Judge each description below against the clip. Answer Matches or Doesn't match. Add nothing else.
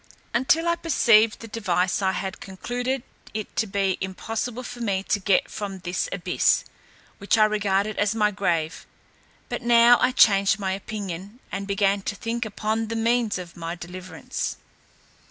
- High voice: Matches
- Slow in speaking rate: Doesn't match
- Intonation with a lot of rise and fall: Doesn't match